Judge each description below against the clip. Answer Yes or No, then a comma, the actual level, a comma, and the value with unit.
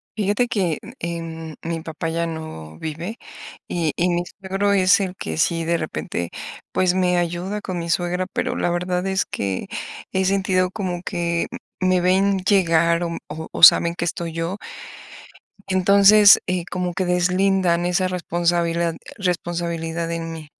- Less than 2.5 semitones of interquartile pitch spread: Yes, narrow, 2.0 semitones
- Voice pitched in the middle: Yes, medium, 175 Hz